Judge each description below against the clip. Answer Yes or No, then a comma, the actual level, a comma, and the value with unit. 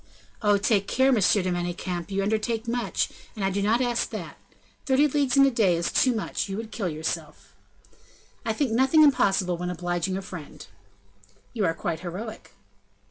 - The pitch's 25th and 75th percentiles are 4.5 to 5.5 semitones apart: Yes, average, 4.9 semitones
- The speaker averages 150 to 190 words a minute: Yes, average, 180 wpm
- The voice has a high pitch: Yes, high, 200 Hz